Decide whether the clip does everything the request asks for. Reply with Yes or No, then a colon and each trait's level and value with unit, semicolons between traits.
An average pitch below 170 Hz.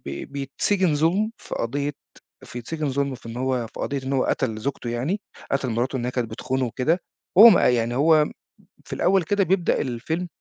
Yes: low, 135 Hz